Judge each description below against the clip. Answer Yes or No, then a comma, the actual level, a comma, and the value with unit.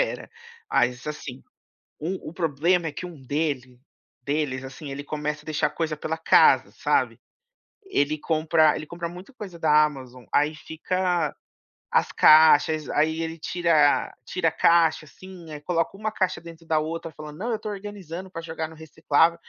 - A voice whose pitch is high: No, medium, 160 Hz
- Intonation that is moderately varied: No, narrow, 2.3 semitones